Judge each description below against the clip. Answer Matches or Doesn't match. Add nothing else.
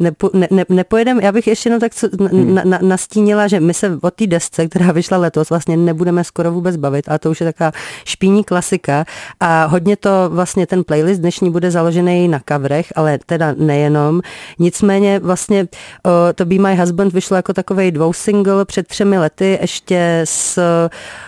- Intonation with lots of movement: Doesn't match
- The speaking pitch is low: Doesn't match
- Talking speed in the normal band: Doesn't match